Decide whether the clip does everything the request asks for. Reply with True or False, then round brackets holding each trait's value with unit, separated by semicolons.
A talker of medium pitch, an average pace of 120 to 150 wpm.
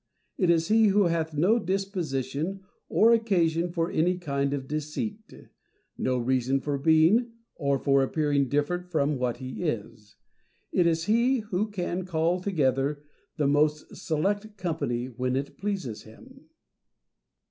True (160 Hz; 140 wpm)